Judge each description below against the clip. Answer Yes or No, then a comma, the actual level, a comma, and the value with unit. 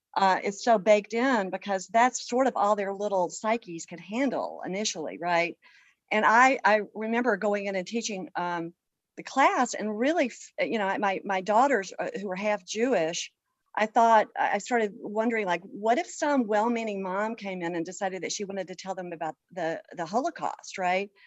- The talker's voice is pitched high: Yes, high, 205 Hz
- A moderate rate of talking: Yes, average, 185 wpm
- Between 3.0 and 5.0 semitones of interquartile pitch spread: Yes, average, 3.7 semitones